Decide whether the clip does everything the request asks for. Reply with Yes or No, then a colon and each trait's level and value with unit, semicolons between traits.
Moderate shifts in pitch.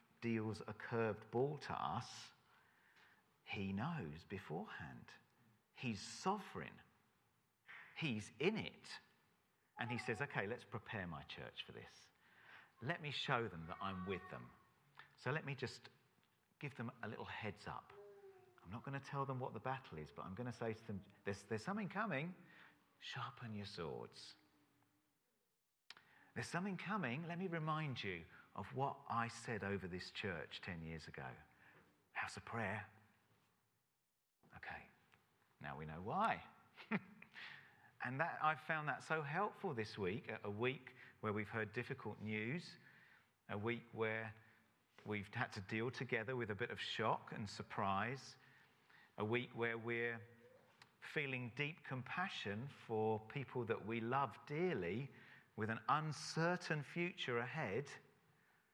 Yes: average, 4.5 semitones